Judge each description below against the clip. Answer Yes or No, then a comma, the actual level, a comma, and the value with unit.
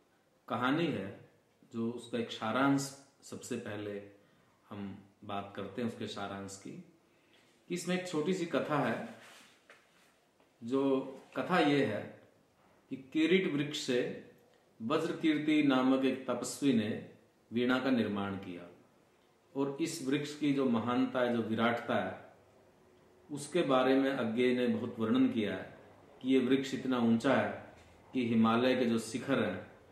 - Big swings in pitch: No, average, 3.5 semitones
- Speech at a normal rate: Yes, average, 145 wpm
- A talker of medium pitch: No, low, 125 Hz